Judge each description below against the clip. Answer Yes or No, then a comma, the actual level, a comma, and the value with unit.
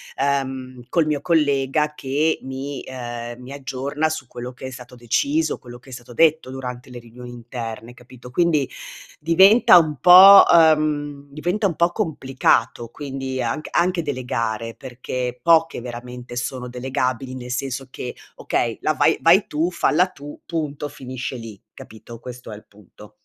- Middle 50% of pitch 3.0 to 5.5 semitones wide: Yes, average, 3.8 semitones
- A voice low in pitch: Yes, low, 130 Hz